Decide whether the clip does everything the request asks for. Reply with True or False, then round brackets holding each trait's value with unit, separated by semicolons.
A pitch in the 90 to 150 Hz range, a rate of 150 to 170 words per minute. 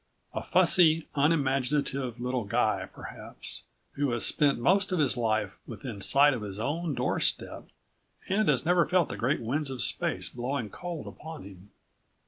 True (140 Hz; 155 wpm)